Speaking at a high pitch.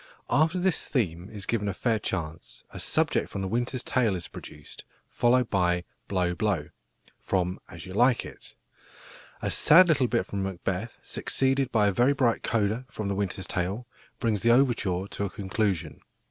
No: low, 105 Hz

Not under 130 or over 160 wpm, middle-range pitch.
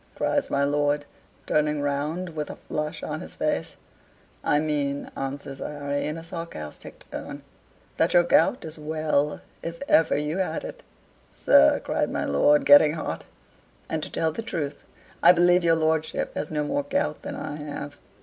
No: average, 170 wpm; medium, 150 Hz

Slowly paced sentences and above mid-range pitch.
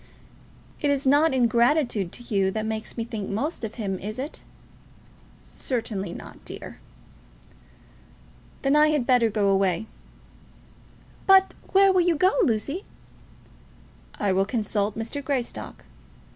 Yes: slow, 130 wpm; high, 235 Hz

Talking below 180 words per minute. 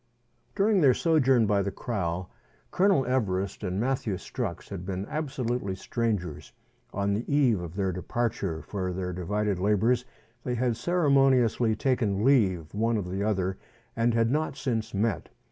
Yes: average, 150 wpm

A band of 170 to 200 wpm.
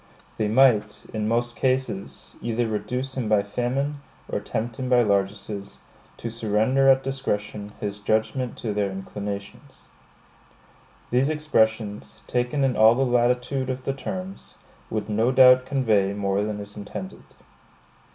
No: average, 140 wpm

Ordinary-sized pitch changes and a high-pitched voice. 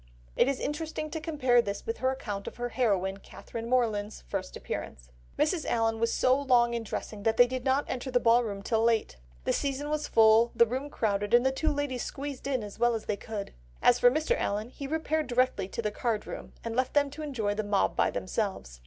Yes: average, 4.0 semitones; high, 240 Hz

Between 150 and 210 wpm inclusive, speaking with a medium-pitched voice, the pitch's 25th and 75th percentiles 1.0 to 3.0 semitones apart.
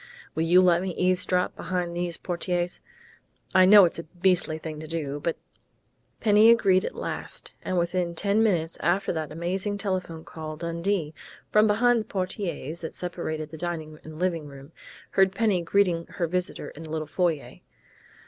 Yes: average, 170 wpm; medium, 175 Hz; narrow, 2.6 semitones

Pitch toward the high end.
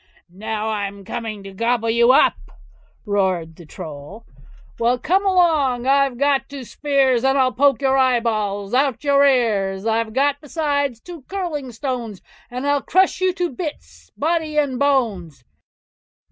Yes: very high, 255 Hz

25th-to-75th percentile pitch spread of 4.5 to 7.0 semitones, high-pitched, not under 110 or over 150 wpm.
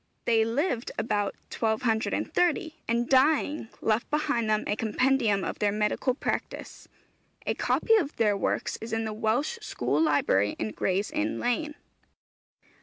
Yes: average, 5.3 semitones; high, 230 Hz; average, 140 wpm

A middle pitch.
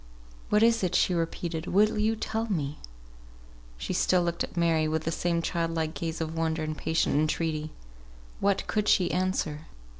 Yes: medium, 165 Hz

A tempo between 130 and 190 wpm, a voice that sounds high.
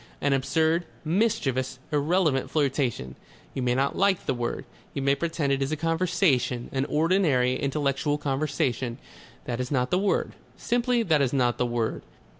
No: average, 160 wpm; medium, 140 Hz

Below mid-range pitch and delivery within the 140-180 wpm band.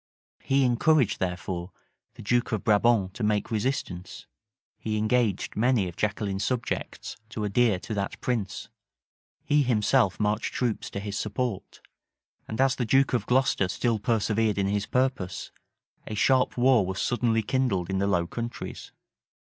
Yes: low, 110 Hz; average, 150 wpm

